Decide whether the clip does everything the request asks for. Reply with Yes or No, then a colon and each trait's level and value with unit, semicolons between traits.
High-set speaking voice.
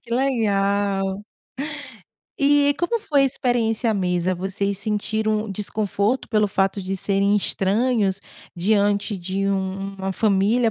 Yes: high, 205 Hz